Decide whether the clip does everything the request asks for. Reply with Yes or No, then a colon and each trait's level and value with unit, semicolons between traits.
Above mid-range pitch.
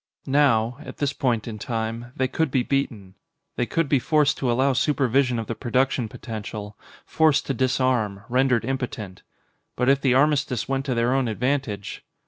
No: low, 125 Hz